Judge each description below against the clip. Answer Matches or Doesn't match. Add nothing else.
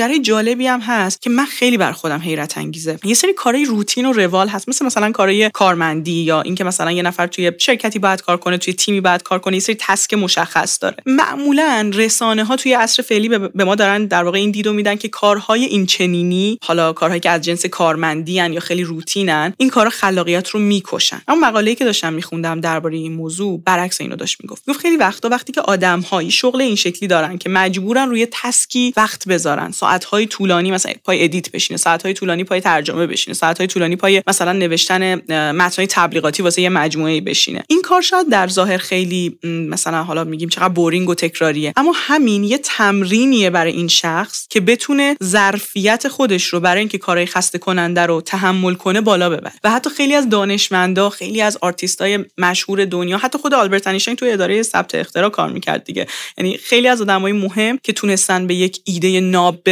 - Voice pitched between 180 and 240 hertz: Matches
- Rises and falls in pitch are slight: Doesn't match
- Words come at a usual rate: Doesn't match